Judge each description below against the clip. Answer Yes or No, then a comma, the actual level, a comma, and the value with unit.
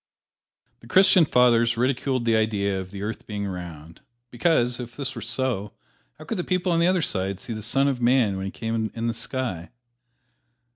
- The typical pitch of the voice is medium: No, low, 115 Hz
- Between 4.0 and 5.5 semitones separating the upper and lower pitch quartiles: Yes, average, 4.5 semitones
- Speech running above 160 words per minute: Yes, average, 195 wpm